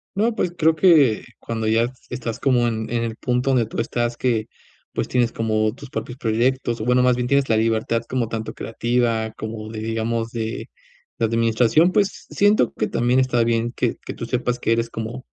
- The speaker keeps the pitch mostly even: Yes, narrow, 2.0 semitones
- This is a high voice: No, low, 115 Hz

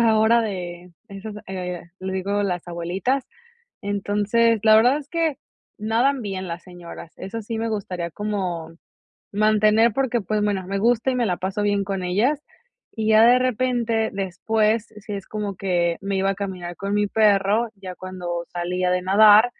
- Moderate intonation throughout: Yes, average, 3.2 semitones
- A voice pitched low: No, high, 205 Hz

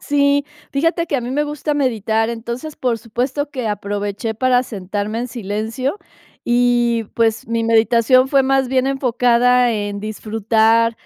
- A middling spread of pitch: Yes, average, 3.0 semitones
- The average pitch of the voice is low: No, high, 235 Hz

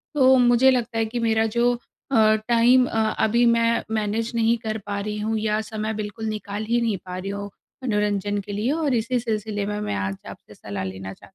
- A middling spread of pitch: No, narrow, 2.3 semitones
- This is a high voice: Yes, high, 220 Hz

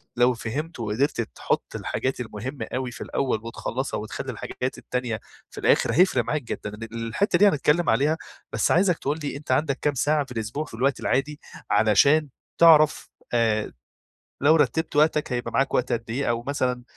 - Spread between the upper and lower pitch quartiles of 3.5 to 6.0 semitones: Yes, average, 4.4 semitones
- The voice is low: Yes, low, 130 Hz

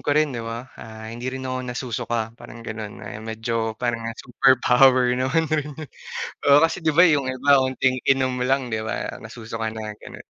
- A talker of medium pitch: No, low, 125 Hz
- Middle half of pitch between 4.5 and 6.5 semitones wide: No, average, 2.7 semitones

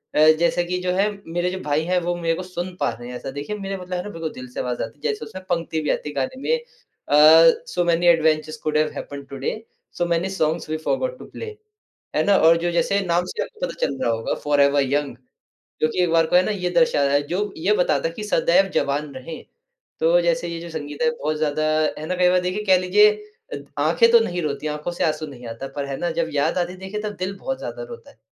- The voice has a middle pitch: Yes, medium, 170 Hz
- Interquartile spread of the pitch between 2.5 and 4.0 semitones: Yes, average, 3.7 semitones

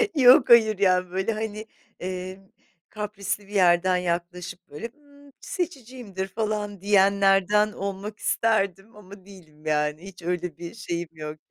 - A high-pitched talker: Yes, high, 195 Hz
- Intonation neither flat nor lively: Yes, average, 3.0 semitones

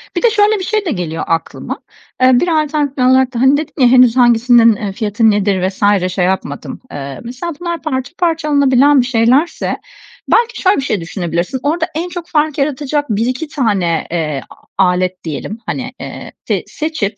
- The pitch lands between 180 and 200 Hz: No, very high, 255 Hz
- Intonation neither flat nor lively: No, wide, 7.2 semitones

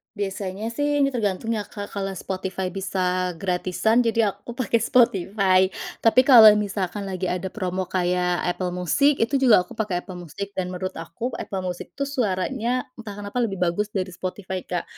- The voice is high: Yes, high, 195 Hz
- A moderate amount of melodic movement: Yes, average, 3.7 semitones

